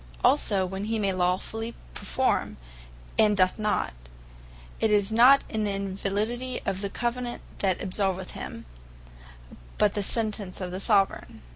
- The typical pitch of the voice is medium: No, high, 205 Hz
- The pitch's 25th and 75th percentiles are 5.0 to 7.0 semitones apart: No, narrow, 2.5 semitones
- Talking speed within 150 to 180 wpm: No, slow, 135 wpm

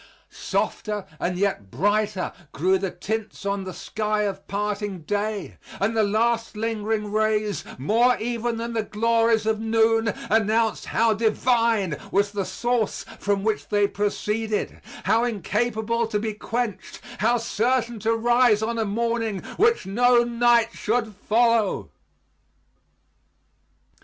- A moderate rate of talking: No, slow, 130 wpm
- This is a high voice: Yes, high, 220 Hz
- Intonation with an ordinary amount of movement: No, narrow, 2.0 semitones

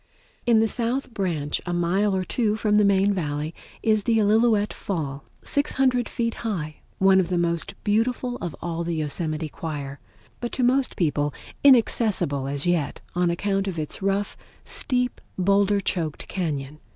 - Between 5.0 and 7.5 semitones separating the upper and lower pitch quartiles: Yes, wide, 5.5 semitones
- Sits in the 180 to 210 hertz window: Yes, high, 190 Hz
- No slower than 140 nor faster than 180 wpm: Yes, average, 160 wpm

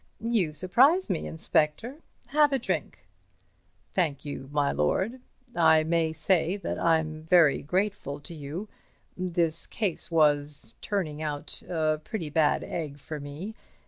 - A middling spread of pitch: Yes, average, 4.1 semitones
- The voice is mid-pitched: Yes, medium, 160 Hz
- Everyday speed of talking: No, slow, 130 wpm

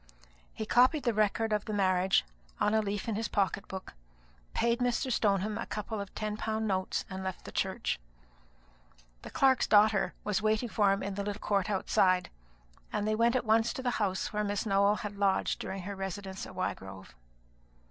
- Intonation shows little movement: Yes, narrow, 2.2 semitones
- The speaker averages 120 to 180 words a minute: No, average, 190 wpm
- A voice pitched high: Yes, high, 205 Hz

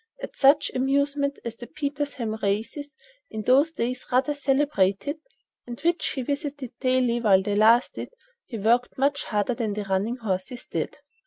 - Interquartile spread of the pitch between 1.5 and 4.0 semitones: No, average, 4.5 semitones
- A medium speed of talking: Yes, average, 155 wpm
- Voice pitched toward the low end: No, very high, 255 Hz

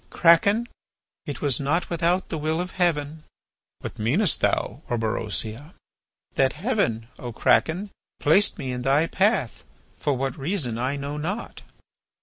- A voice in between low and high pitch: Yes, medium, 150 Hz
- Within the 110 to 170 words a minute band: Yes, slow, 135 wpm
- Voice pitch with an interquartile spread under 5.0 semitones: No, wide, 5.5 semitones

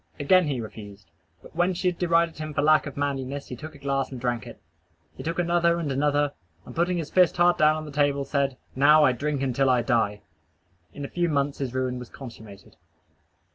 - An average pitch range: Yes, average, 3.6 semitones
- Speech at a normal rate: No, fast, 215 wpm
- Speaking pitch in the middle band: Yes, medium, 145 Hz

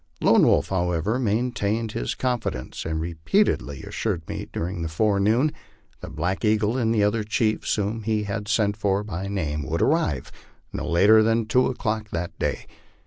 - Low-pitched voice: Yes, low, 105 Hz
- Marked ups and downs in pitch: No, average, 4.3 semitones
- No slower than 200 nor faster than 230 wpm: No, average, 170 wpm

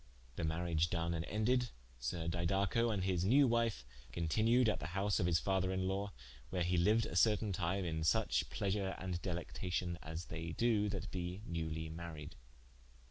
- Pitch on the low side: Yes, very low, 90 Hz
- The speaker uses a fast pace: No, average, 175 wpm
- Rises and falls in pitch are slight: No, average, 3.5 semitones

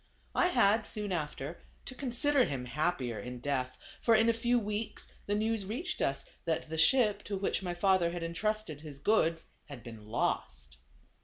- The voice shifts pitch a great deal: Yes, wide, 7.5 semitones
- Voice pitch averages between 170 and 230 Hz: Yes, medium, 185 Hz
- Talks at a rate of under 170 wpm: No, average, 175 wpm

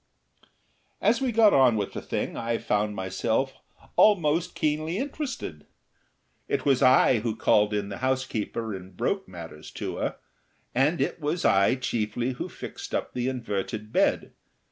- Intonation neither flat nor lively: No, wide, 6.3 semitones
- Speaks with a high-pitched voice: No, low, 120 Hz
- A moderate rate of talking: Yes, average, 150 wpm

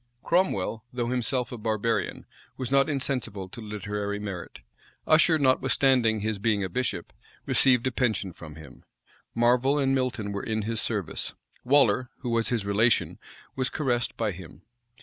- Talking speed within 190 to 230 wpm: No, average, 150 wpm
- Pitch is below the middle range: Yes, low, 115 Hz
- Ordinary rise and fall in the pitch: Yes, average, 3.9 semitones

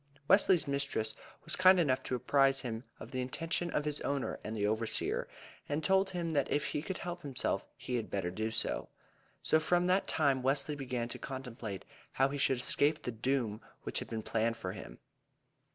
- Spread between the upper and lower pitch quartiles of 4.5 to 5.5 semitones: Yes, average, 5.1 semitones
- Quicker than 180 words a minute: Yes, average, 195 wpm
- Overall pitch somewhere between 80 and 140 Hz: Yes, low, 135 Hz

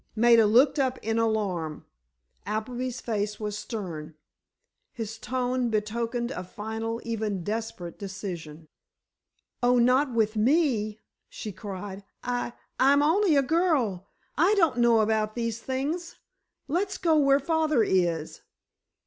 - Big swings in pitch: No, average, 4.0 semitones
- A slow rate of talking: Yes, slow, 115 wpm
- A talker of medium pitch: No, high, 230 Hz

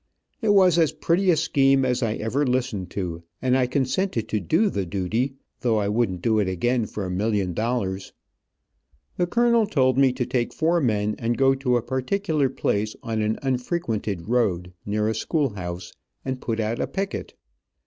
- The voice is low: Yes, low, 120 Hz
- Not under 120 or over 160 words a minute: No, average, 185 wpm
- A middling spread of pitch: Yes, average, 4.6 semitones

